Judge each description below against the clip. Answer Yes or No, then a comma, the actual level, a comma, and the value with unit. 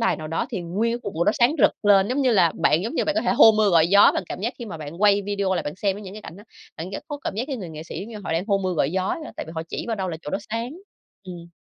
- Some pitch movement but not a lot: Yes, average, 4.6 semitones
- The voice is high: Yes, high, 195 Hz